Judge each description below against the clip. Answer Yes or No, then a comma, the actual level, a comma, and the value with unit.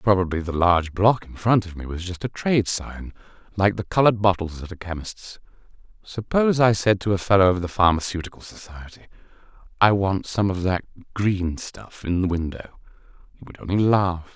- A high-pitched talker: No, very low, 95 Hz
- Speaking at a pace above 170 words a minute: Yes, average, 185 wpm